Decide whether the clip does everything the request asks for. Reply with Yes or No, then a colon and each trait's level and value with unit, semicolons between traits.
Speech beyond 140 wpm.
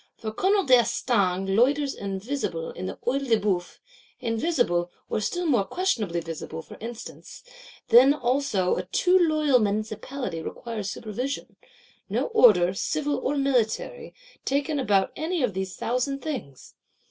No: slow, 135 wpm